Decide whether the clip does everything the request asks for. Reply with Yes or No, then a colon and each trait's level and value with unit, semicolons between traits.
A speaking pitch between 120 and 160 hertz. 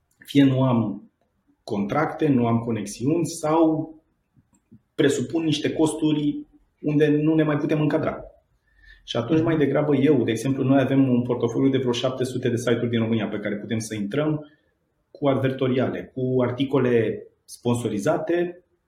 Yes: low, 135 Hz